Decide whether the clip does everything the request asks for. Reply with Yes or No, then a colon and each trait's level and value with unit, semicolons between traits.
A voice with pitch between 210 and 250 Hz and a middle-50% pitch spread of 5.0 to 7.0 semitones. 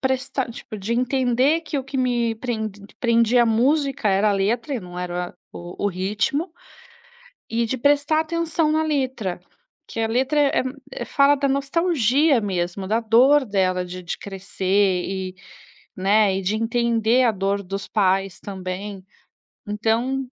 Yes: high, 230 Hz; wide, 5.4 semitones